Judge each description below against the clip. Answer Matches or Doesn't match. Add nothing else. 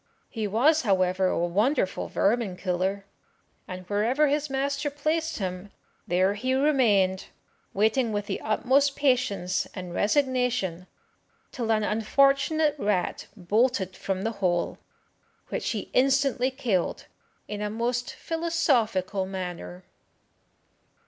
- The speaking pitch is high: Matches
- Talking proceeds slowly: Matches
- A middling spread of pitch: Doesn't match